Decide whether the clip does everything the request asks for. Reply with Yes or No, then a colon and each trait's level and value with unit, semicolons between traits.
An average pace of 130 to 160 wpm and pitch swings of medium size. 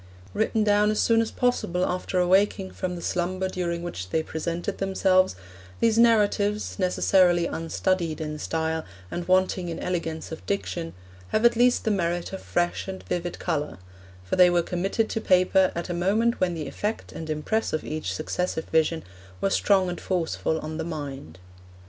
No: average, 175 wpm; average, 3.1 semitones